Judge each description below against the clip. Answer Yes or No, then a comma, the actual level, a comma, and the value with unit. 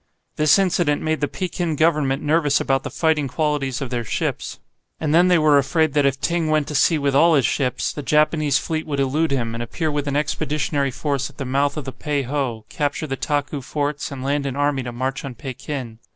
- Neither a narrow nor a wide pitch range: No, narrow, 2.3 semitones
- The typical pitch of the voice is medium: Yes, medium, 145 Hz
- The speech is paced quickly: Yes, fast, 225 wpm